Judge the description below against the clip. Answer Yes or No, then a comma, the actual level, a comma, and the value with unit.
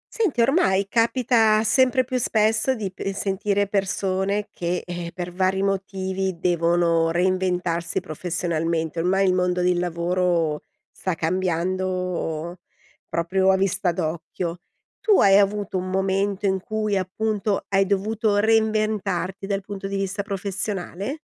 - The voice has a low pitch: No, high, 190 Hz